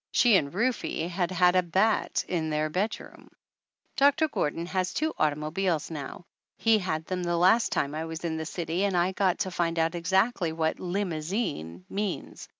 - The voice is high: No, medium, 175 Hz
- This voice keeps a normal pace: Yes, average, 175 wpm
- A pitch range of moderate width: Yes, average, 3.3 semitones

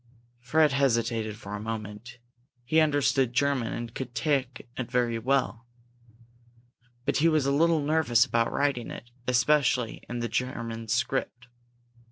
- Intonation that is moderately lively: Yes, average, 3.4 semitones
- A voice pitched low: Yes, low, 125 Hz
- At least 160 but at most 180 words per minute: No, average, 140 wpm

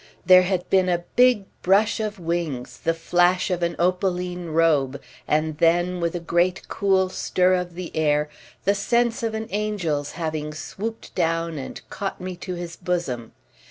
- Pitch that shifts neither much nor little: No, narrow, 2.3 semitones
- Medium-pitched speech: Yes, medium, 175 Hz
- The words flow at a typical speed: Yes, average, 165 wpm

